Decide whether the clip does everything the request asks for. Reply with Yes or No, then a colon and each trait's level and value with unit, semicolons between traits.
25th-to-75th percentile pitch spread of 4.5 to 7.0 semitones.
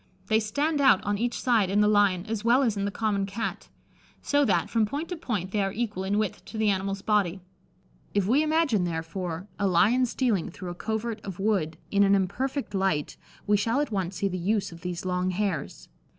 No: average, 3.3 semitones